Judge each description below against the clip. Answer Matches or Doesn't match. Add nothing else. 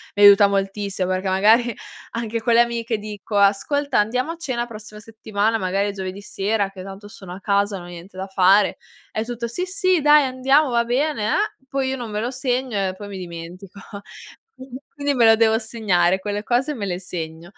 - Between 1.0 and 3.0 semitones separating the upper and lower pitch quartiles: Doesn't match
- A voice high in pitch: Matches